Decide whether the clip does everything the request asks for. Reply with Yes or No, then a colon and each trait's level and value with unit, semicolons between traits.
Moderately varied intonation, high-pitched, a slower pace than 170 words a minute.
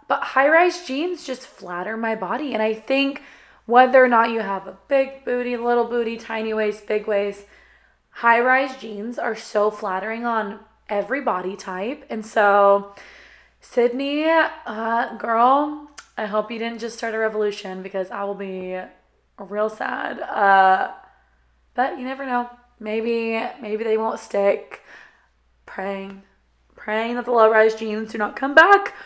Yes: average, 3.5 semitones; high, 225 Hz; average, 155 wpm